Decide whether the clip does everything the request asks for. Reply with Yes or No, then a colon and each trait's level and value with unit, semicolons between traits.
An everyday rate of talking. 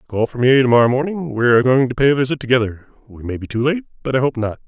No: fast, 295 wpm